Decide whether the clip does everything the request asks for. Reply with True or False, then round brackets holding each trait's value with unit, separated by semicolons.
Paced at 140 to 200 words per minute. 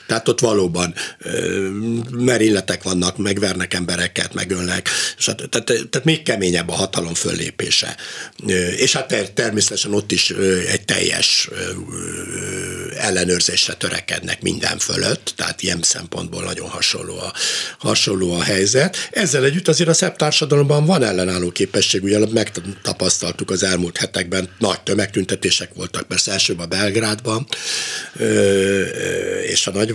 False (115 wpm)